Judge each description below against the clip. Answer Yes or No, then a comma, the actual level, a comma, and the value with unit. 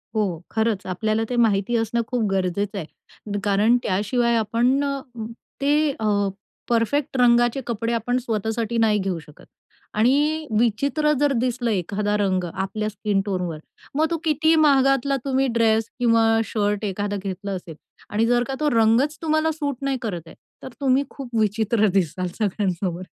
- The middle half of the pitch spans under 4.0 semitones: No, average, 4.4 semitones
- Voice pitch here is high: Yes, high, 225 Hz